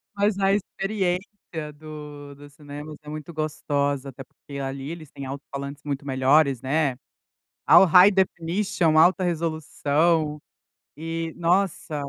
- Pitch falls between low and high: Yes, medium, 155 Hz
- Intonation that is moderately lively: Yes, average, 3.2 semitones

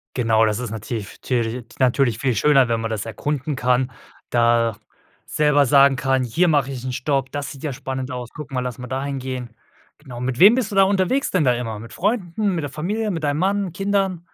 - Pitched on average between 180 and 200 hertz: No, low, 135 Hz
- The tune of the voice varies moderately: Yes, average, 4.7 semitones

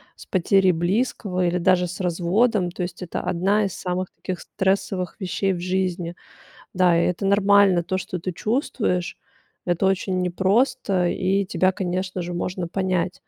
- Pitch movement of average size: No, narrow, 1.5 semitones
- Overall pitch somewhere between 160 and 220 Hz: Yes, medium, 185 Hz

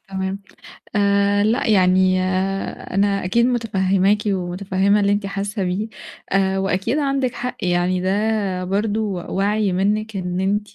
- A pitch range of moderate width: No, narrow, 1.9 semitones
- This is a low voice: No, high, 195 Hz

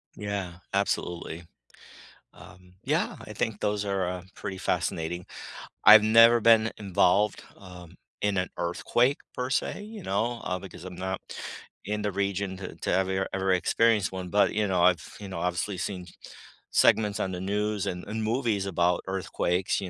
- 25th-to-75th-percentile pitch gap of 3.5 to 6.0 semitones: No, narrow, 2.6 semitones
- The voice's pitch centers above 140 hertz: No, very low, 95 Hz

